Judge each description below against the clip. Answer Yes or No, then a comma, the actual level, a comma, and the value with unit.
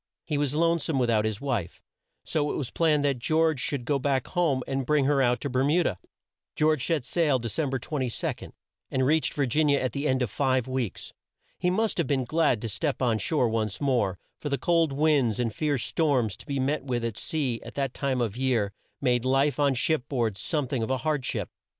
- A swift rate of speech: Yes, fast, 235 wpm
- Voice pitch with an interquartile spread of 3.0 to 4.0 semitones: Yes, average, 3.5 semitones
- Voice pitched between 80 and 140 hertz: Yes, low, 135 Hz